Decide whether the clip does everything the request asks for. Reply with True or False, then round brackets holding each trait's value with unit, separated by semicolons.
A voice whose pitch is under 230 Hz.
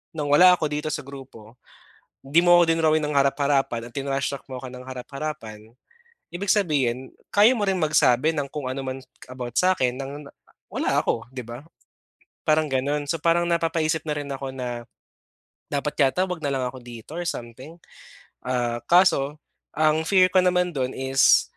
True (140 Hz)